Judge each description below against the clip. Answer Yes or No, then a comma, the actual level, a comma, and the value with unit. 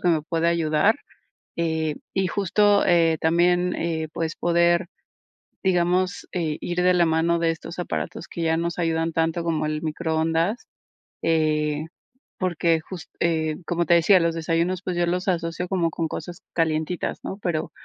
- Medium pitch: Yes, medium, 170 Hz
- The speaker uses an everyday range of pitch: No, narrow, 1.6 semitones